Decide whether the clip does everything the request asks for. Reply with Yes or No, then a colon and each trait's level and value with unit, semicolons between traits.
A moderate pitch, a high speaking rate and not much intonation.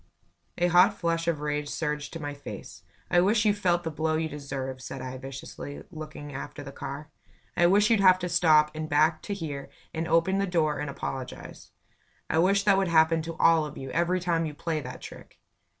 No: medium, 160 Hz; fast, 210 wpm; average, 3.1 semitones